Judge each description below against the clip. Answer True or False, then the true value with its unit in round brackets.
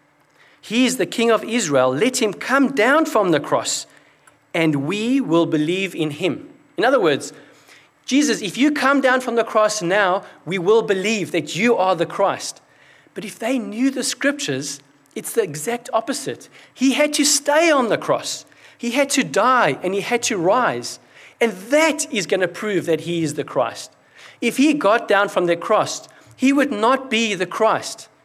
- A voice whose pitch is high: True (225 Hz)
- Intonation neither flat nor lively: False (6.6 semitones)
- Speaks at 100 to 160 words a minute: False (190 wpm)